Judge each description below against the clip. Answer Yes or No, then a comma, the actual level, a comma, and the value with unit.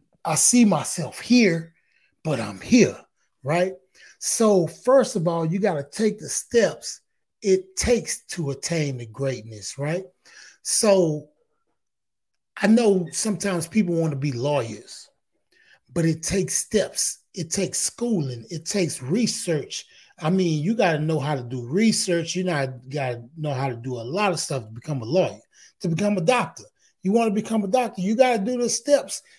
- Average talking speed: Yes, average, 175 wpm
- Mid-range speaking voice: Yes, medium, 180 Hz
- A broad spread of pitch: Yes, wide, 5.9 semitones